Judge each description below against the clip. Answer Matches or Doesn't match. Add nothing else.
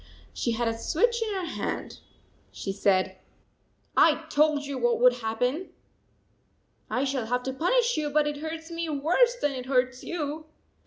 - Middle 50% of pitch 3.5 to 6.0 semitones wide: Matches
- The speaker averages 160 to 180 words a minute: Matches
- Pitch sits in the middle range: Doesn't match